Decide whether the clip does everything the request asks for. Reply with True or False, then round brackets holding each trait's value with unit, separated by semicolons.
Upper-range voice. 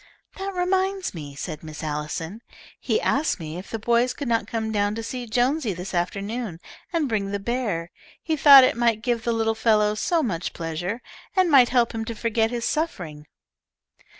True (225 Hz)